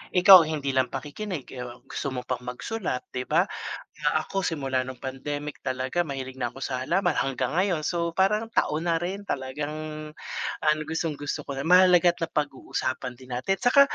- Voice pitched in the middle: Yes, medium, 150 Hz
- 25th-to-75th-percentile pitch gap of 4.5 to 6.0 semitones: Yes, average, 5.1 semitones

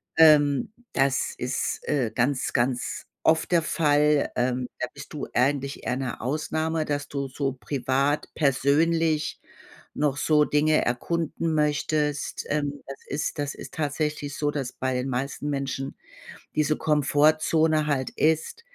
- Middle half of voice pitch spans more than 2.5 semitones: No, narrow, 2.2 semitones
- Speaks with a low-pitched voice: No, medium, 145 Hz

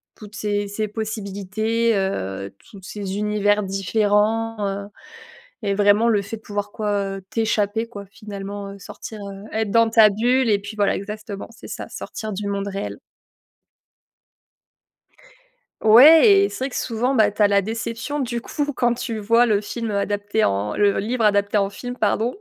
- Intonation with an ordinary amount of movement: No, narrow, 2.1 semitones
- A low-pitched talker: No, high, 210 Hz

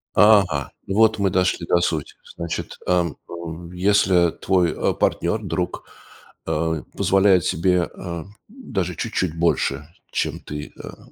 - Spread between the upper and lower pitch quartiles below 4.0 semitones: Yes, average, 2.7 semitones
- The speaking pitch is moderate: No, very low, 90 Hz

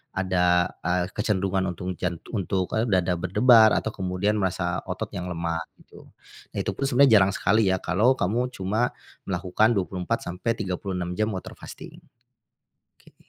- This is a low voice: Yes, very low, 95 Hz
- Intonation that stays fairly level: No, average, 3.2 semitones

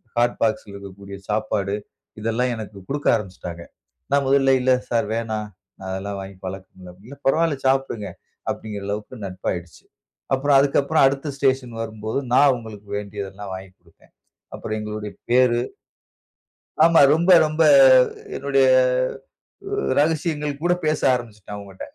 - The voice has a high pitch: No, low, 110 Hz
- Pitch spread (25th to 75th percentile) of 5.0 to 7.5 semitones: Yes, average, 5.3 semitones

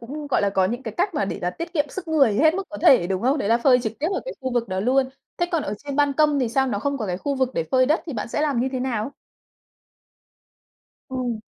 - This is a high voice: Yes, very high, 260 Hz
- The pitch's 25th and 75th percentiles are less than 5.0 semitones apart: Yes, average, 4.4 semitones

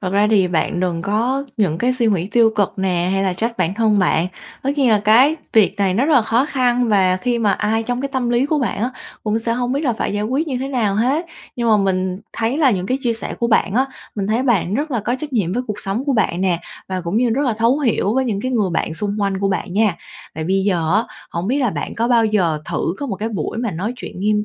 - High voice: Yes, high, 220 Hz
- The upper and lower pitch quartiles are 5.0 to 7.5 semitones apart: No, average, 4.3 semitones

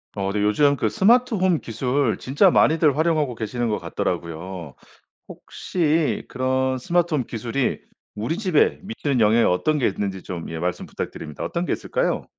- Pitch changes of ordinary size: No, wide, 7.7 semitones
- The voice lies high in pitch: No, low, 130 Hz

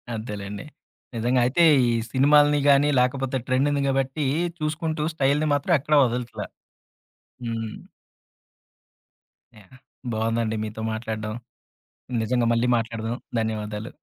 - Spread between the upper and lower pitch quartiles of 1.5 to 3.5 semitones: No, average, 4.1 semitones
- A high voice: No, low, 125 Hz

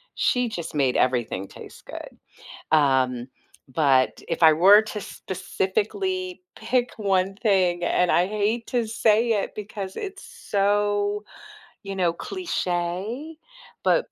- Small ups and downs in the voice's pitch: No, average, 4.6 semitones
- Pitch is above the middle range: Yes, high, 200 Hz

